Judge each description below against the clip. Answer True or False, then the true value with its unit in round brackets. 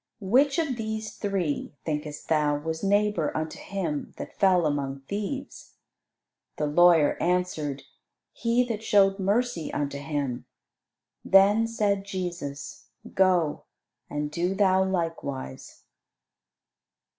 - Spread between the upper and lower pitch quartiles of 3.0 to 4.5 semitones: False (5.3 semitones)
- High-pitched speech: False (180 Hz)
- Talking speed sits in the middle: False (110 wpm)